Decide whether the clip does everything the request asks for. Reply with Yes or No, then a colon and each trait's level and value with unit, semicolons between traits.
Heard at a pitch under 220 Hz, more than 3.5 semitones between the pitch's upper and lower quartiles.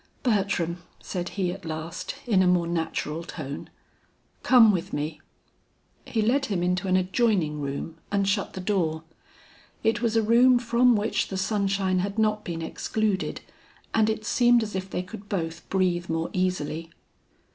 Yes: high, 190 Hz; average, 4.2 semitones